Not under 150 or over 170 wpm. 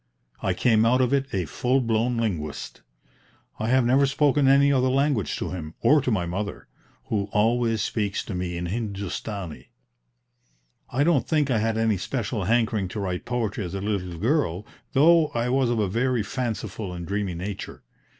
No: average, 180 wpm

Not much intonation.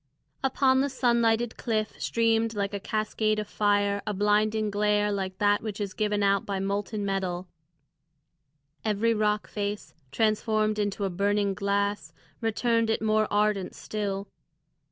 Yes: narrow, 1.3 semitones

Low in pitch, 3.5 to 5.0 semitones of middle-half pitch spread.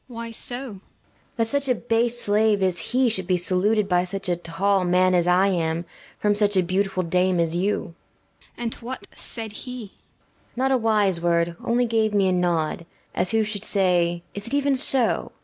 No: high, 200 Hz; average, 4.2 semitones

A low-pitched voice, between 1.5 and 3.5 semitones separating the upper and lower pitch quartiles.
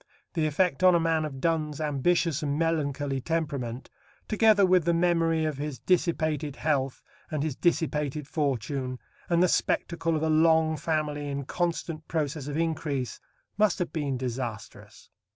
No: medium, 155 Hz; average, 2.8 semitones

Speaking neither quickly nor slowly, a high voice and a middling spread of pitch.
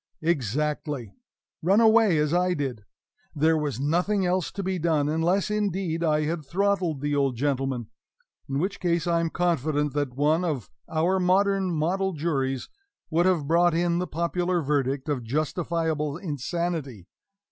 No: average, 150 wpm; medium, 160 Hz; average, 3.6 semitones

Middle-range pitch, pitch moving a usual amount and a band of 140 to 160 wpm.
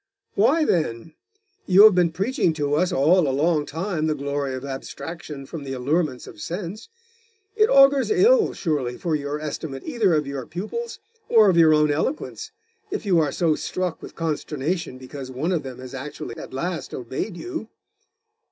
No: medium, 160 Hz; average, 4.9 semitones; average, 175 wpm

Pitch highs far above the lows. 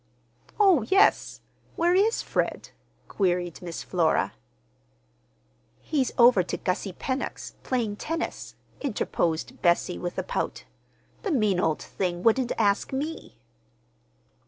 Yes: wide, 8.6 semitones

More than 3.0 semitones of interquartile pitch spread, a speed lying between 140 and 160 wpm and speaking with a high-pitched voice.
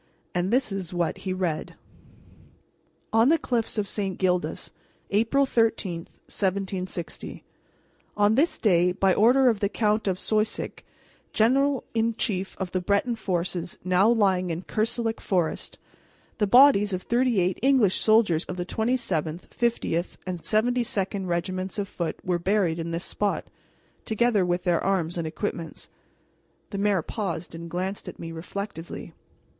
Yes: average, 3.9 semitones; average, 145 wpm; high, 195 Hz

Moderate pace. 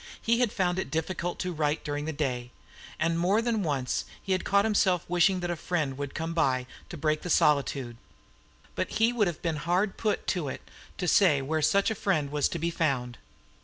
No: fast, 210 wpm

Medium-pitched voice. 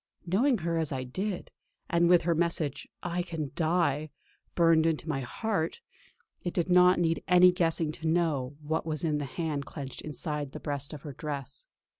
Yes: medium, 160 Hz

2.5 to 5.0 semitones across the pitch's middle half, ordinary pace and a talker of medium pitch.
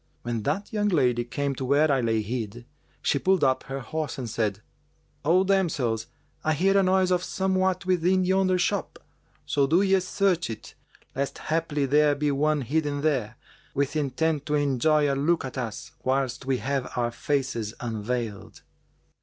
No: wide, 5.6 semitones; average, 170 wpm; medium, 145 Hz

